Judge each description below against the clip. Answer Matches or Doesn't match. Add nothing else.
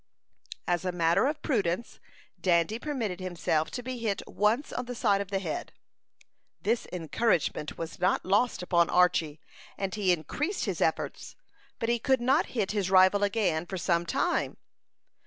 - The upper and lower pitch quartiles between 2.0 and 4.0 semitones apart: Doesn't match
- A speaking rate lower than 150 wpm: Doesn't match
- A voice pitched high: Matches